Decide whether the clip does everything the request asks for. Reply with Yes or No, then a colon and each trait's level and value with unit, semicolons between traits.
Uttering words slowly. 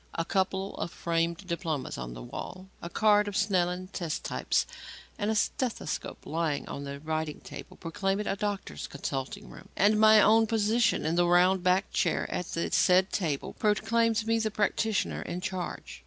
No: average, 175 wpm